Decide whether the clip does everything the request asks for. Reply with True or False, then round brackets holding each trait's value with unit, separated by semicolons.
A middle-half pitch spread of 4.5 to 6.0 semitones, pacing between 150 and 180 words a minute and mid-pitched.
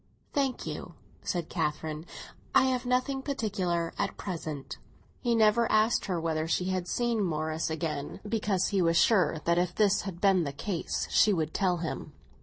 True (4.9 semitones; 170 wpm; 180 Hz)